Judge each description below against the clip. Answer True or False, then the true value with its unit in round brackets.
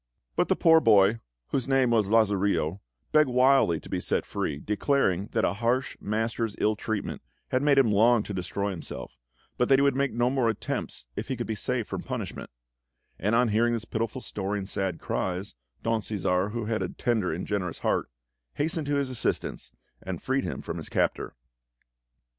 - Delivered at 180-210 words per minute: True (190 wpm)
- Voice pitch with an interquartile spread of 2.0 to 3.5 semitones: False (4.3 semitones)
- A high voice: False (110 Hz)